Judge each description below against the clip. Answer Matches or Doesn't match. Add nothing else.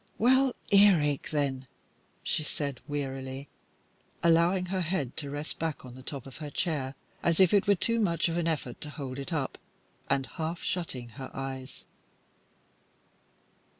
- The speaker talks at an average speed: Matches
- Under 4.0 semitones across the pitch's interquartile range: Doesn't match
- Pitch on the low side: Doesn't match